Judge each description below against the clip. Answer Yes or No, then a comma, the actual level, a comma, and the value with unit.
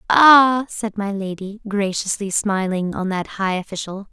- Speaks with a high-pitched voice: Yes, high, 205 Hz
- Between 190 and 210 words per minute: No, average, 145 wpm